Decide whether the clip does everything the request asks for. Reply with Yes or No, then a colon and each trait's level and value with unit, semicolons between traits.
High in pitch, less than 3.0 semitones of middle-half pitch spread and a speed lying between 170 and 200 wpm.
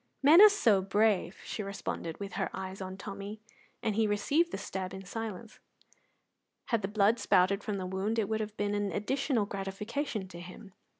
Yes: high, 205 Hz; narrow, 2.4 semitones; average, 185 wpm